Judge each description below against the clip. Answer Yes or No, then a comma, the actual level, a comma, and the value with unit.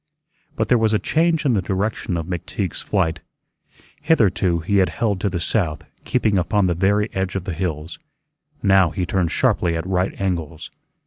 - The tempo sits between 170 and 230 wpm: Yes, average, 180 wpm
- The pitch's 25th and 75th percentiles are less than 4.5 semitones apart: Yes, average, 3.3 semitones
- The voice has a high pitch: No, very low, 95 Hz